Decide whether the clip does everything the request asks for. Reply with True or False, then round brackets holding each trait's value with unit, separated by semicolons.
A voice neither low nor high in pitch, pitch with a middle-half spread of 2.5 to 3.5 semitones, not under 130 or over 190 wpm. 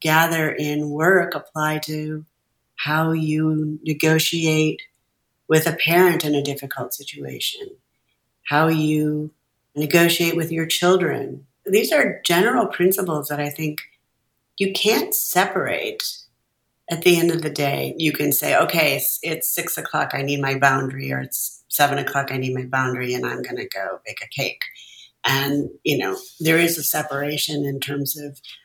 True (155 Hz; 2.9 semitones; 155 wpm)